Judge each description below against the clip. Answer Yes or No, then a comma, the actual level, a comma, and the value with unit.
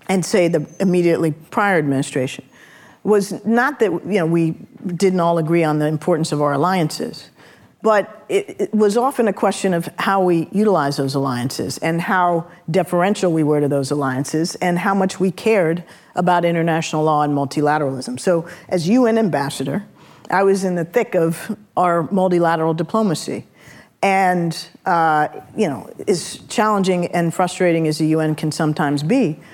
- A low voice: No, medium, 175 Hz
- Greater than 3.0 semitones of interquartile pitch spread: Yes, average, 3.8 semitones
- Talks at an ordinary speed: Yes, average, 160 wpm